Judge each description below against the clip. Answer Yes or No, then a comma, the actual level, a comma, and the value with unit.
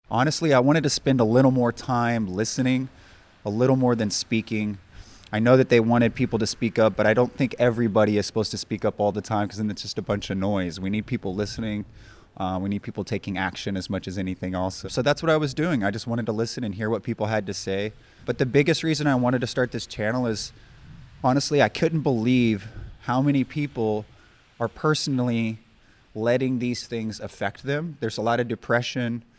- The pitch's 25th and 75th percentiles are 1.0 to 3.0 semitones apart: No, average, 3.4 semitones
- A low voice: Yes, low, 115 Hz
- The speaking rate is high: Yes, fast, 220 wpm